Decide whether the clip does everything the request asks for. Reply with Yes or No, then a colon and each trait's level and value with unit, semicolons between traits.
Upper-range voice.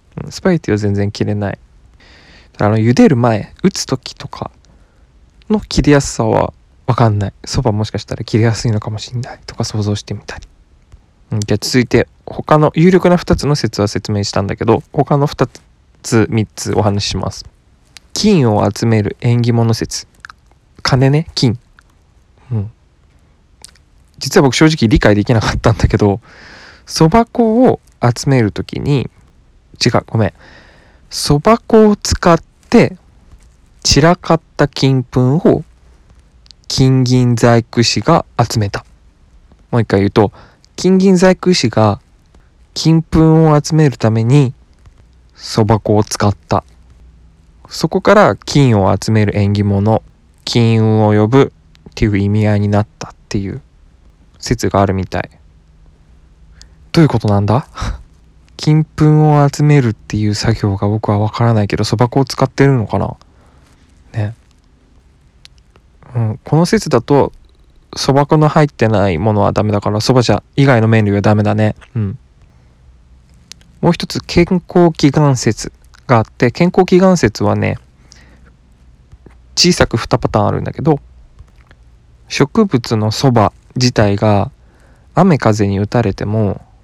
No: low, 110 Hz